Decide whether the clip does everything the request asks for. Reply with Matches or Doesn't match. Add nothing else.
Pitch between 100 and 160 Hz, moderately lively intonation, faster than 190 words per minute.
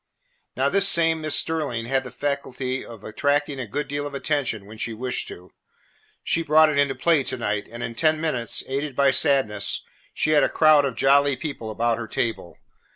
Matches